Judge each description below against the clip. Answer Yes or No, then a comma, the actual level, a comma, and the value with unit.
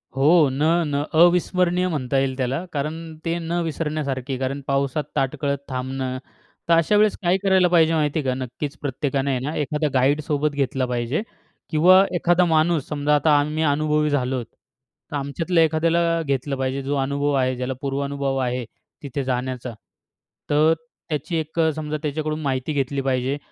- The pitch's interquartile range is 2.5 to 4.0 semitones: Yes, average, 3.0 semitones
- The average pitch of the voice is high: No, medium, 145 Hz